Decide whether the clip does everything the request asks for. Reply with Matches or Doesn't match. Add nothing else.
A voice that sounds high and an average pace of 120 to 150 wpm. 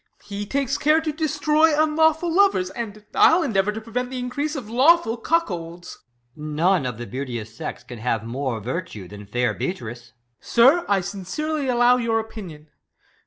Doesn't match